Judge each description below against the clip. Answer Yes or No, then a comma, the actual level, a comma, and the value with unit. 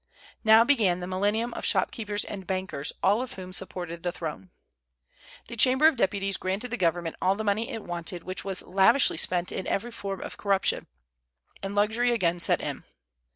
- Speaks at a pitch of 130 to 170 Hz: No, high, 195 Hz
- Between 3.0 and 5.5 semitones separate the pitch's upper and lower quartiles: Yes, average, 3.5 semitones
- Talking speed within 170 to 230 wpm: Yes, average, 180 wpm